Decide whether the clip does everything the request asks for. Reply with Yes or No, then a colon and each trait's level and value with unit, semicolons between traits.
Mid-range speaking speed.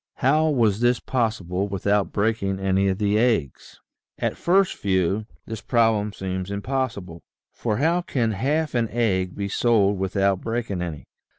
Yes: average, 150 wpm